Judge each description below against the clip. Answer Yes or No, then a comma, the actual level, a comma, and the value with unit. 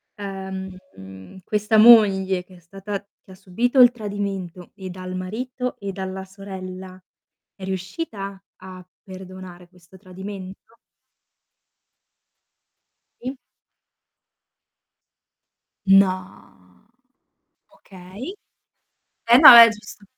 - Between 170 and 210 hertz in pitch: Yes, high, 190 Hz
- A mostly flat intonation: Yes, narrow, 2.0 semitones